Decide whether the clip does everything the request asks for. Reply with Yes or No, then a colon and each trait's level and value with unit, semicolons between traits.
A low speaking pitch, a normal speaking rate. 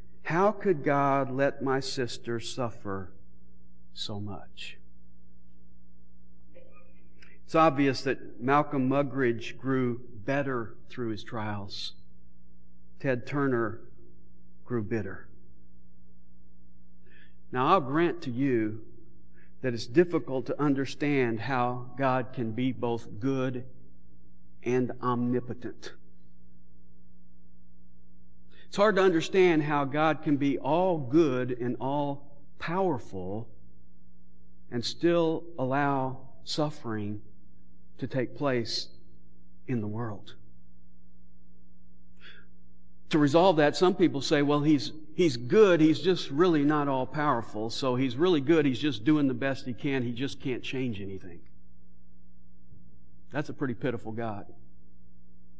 No: low, 115 Hz; slow, 110 wpm